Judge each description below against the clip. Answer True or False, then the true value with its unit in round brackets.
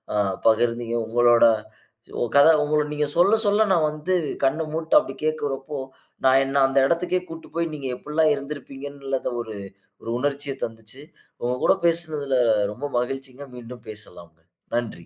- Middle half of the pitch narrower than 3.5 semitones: False (4.1 semitones)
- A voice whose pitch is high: False (135 Hz)